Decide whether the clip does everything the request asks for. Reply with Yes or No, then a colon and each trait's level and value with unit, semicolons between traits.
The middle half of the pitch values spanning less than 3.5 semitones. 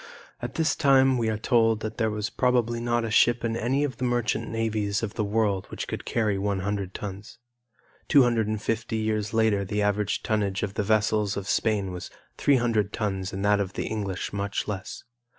Yes: narrow, 2.4 semitones